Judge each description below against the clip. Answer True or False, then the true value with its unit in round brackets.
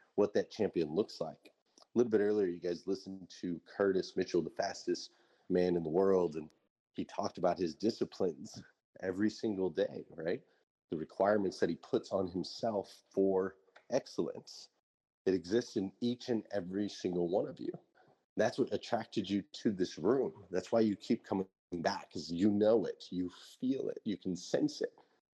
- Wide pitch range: False (3.8 semitones)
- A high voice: False (95 Hz)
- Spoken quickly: False (175 wpm)